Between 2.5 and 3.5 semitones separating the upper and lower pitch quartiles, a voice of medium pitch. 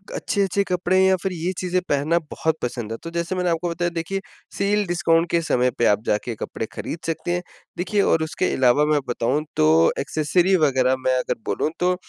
No: average, 4.8 semitones; medium, 165 Hz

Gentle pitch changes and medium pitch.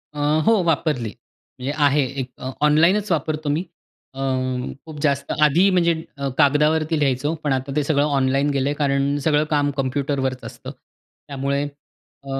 Yes: narrow, 2.2 semitones; medium, 145 Hz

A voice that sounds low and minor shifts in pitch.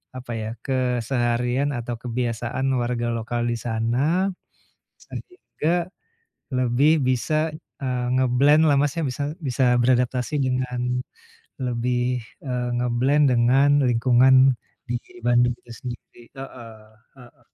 Yes: low, 125 Hz; narrow, 2.0 semitones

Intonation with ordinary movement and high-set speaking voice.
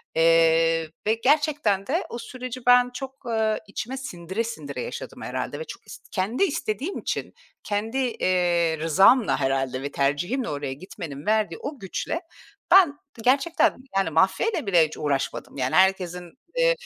No: wide, 7.7 semitones; high, 195 Hz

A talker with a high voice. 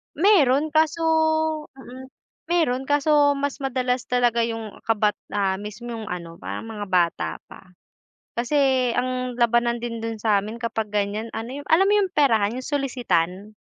Yes: high, 240 Hz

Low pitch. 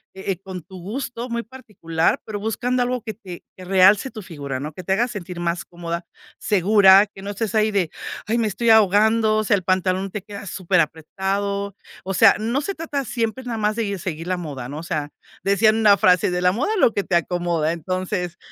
No: high, 195 Hz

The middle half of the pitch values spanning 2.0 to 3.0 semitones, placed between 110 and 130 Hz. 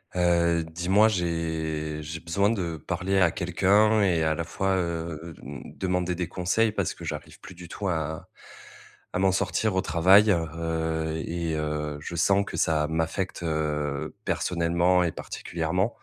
No: narrow, 2.6 semitones; very low, 85 Hz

